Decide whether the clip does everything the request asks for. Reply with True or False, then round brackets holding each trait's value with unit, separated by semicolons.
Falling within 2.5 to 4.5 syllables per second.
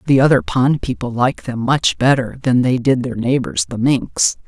False (4.8 syllables/s)